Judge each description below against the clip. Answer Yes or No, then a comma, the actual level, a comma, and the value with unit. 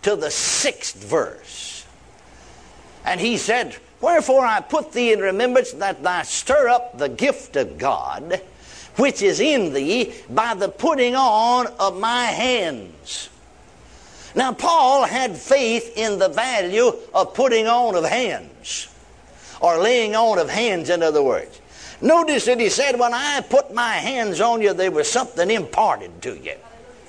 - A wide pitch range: Yes, wide, 6.2 semitones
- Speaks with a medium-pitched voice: No, high, 245 Hz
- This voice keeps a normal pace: Yes, average, 155 wpm